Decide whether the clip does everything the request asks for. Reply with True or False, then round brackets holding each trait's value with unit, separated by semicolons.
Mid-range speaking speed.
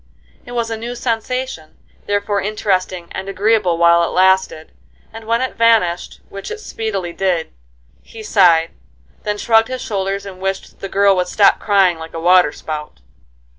True (165 wpm)